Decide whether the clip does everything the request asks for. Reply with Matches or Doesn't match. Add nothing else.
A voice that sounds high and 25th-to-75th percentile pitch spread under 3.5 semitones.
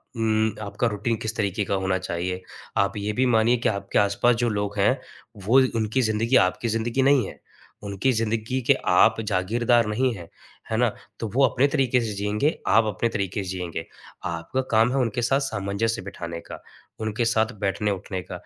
Doesn't match